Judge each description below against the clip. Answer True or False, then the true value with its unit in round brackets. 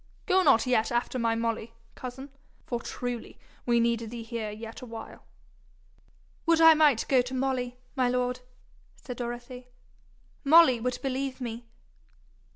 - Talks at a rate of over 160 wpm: False (145 wpm)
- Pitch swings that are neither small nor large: False (2.1 semitones)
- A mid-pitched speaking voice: False (245 Hz)